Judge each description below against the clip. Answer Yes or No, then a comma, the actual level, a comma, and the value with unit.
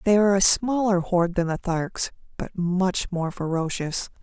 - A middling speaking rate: Yes, average, 170 wpm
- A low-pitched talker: No, medium, 185 Hz